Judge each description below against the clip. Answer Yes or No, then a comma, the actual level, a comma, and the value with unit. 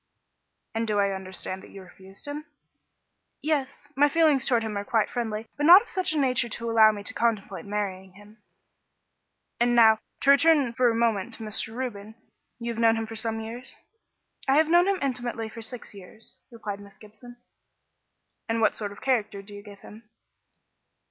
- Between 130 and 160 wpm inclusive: No, average, 190 wpm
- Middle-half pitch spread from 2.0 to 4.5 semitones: Yes, average, 3.4 semitones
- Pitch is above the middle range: Yes, high, 225 Hz